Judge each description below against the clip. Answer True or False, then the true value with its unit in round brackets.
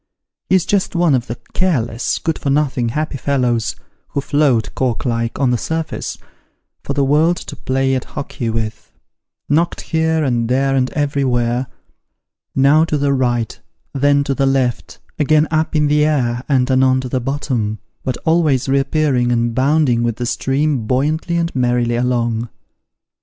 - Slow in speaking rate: False (165 wpm)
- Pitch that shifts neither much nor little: True (3.6 semitones)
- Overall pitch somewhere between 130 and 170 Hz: True (135 Hz)